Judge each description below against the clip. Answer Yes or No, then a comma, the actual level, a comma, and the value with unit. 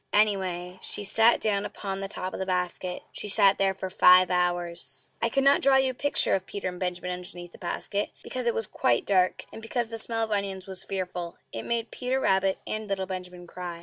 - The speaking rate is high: Yes, fast, 215 wpm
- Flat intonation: No, average, 3.3 semitones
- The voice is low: No, high, 190 Hz